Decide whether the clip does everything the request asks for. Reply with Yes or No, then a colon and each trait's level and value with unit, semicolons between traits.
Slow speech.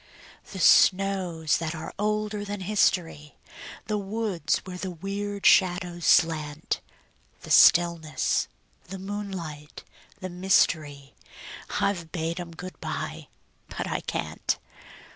Yes: slow, 110 wpm